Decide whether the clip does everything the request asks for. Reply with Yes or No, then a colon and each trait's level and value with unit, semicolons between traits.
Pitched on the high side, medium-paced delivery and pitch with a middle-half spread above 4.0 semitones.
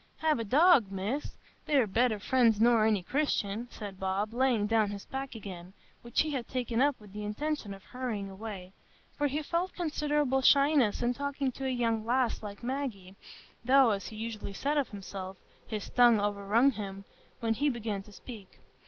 Yes: high, 230 Hz; average, 180 wpm; average, 4.7 semitones